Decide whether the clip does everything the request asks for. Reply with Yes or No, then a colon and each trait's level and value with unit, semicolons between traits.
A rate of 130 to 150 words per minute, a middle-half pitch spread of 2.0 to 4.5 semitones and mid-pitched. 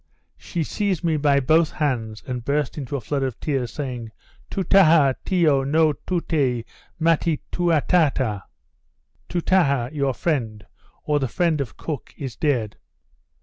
Yes: slow, 135 wpm; average, 4.2 semitones; medium, 145 Hz